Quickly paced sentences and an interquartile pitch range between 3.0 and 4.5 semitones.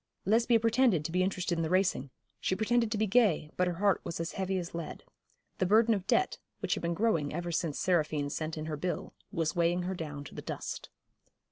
Yes: fast, 225 wpm; average, 4.1 semitones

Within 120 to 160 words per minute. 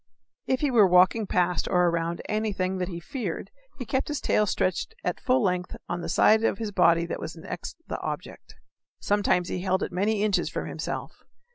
No: average, 200 wpm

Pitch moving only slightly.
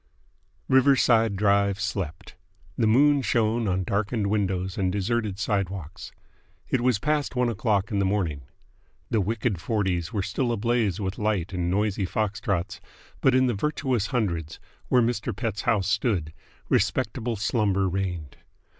No: average, 3.6 semitones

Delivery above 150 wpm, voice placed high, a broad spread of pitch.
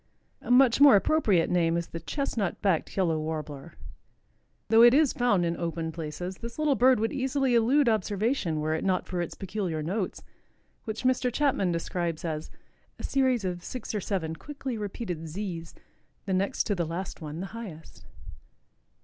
Yes: average, 170 wpm; high, 195 Hz; wide, 6.3 semitones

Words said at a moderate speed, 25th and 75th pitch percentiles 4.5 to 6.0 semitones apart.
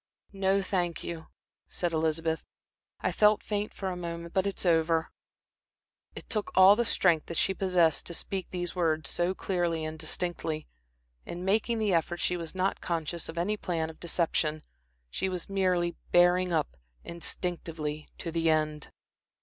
No: average, 165 wpm; narrow, 2.5 semitones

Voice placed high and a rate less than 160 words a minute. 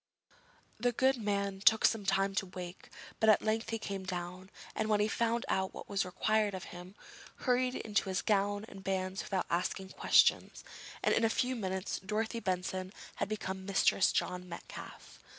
No: high, 195 Hz; average, 175 wpm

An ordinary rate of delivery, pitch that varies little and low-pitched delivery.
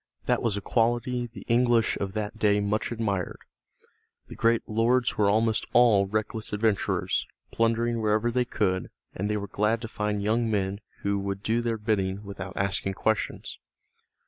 Yes: average, 165 wpm; narrow, 2.3 semitones; low, 110 Hz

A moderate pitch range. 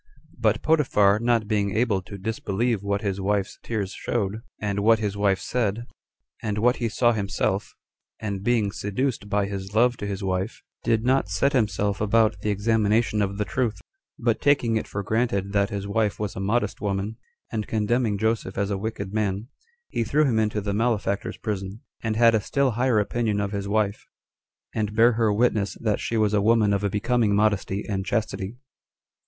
No: narrow, 2.3 semitones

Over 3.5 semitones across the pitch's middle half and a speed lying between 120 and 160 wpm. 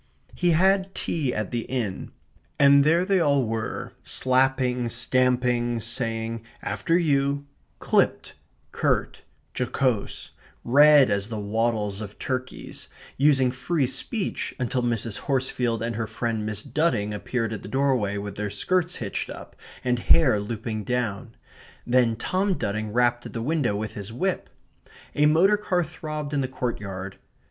Yes: average, 4.3 semitones; average, 145 wpm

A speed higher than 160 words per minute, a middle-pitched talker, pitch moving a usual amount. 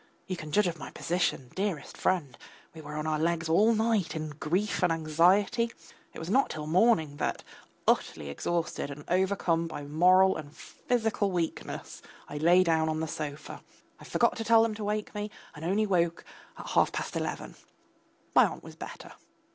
Yes: average, 180 wpm; medium, 170 Hz; average, 4.6 semitones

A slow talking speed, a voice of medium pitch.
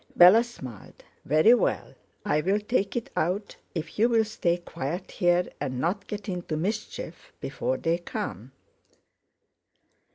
Yes: slow, 125 wpm; medium, 180 Hz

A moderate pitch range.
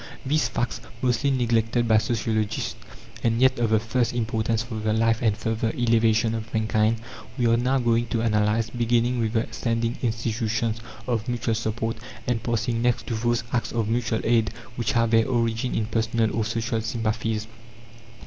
No: narrow, 1.2 semitones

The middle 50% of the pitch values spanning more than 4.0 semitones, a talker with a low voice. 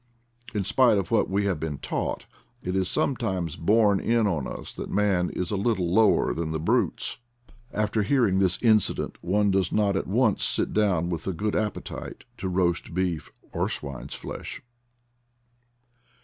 No: average, 3.3 semitones; very low, 95 Hz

